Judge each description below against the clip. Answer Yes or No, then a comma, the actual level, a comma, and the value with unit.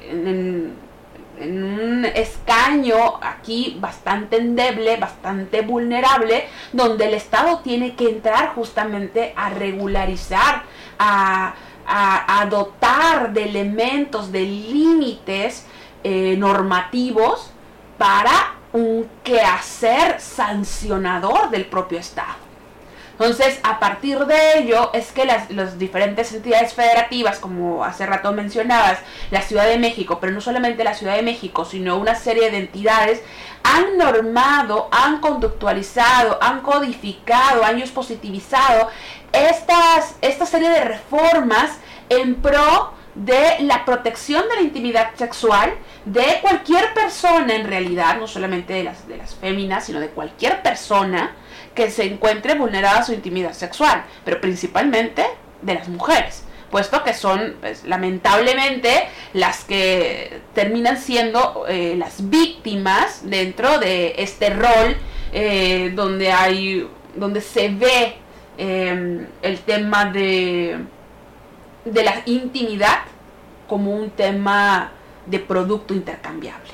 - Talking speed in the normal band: No, slow, 120 wpm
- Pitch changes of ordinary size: Yes, average, 4.4 semitones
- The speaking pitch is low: No, high, 225 Hz